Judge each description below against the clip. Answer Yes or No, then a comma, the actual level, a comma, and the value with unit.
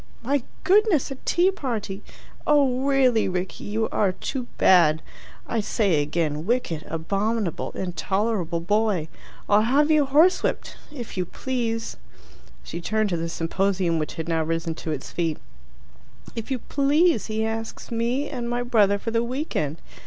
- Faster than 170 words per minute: No, average, 150 wpm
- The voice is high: Yes, high, 220 Hz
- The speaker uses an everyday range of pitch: No, wide, 6.7 semitones